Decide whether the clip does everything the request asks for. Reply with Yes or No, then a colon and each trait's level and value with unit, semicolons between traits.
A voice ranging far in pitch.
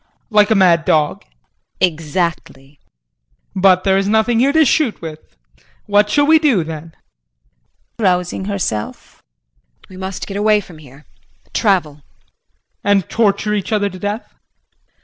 No: average, 4.8 semitones